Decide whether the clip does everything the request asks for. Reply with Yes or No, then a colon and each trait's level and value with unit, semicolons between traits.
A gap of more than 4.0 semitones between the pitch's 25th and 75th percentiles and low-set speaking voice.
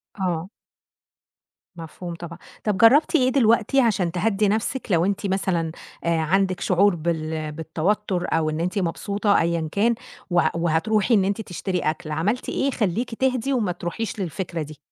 No: average, 4.4 semitones; medium, 185 Hz